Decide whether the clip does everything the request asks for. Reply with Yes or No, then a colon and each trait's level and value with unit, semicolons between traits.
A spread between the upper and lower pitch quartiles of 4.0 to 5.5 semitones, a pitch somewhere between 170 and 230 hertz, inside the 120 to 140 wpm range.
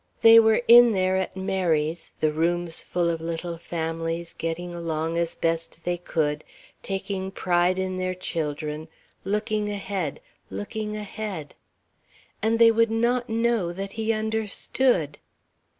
Yes: average, 4.5 semitones; medium, 185 Hz; slow, 135 wpm